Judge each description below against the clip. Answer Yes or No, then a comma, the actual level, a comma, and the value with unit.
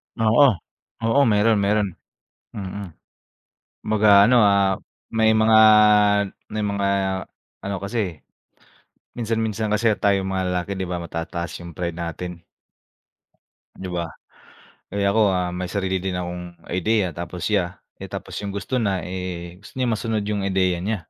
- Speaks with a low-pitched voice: Yes, low, 100 Hz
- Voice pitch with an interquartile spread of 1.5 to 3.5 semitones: Yes, average, 3.1 semitones